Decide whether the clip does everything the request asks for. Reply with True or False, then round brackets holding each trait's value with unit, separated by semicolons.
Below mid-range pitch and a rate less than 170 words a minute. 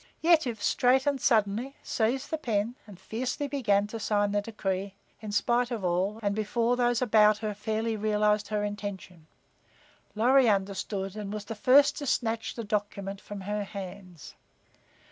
False (210 Hz; 155 wpm)